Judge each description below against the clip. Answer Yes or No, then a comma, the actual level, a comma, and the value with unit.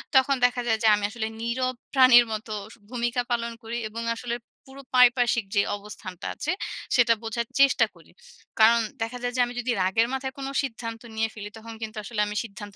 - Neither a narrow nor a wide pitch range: No, narrow, 2.1 semitones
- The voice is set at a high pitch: Yes, high, 235 Hz